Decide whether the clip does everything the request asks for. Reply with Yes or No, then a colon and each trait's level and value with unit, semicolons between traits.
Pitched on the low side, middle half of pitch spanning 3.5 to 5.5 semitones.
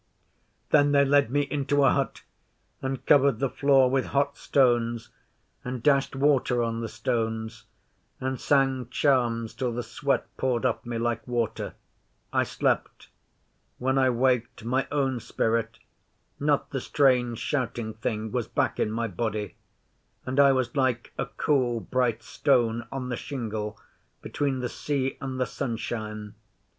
No: low, 125 Hz; average, 2.9 semitones